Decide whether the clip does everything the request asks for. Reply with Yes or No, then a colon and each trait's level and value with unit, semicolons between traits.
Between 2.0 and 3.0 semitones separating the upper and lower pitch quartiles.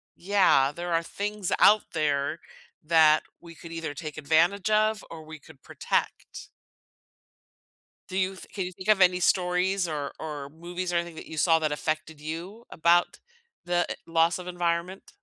Yes: average, 2.7 semitones